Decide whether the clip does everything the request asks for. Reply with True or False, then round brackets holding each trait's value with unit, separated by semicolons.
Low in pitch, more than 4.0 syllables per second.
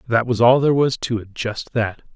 True (120 Hz; 5.3 syllables/s)